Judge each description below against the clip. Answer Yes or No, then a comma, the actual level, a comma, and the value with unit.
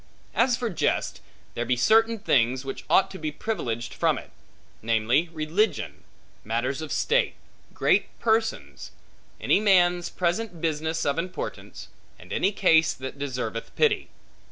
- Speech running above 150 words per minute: No, slow, 135 wpm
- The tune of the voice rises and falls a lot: Yes, wide, 8.1 semitones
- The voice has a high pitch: No, medium, 165 Hz